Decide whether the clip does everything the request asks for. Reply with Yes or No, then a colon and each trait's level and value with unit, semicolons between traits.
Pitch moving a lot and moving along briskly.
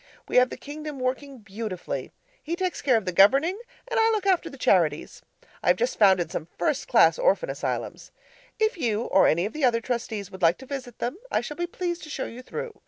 Yes: wide, 8.4 semitones; fast, 225 wpm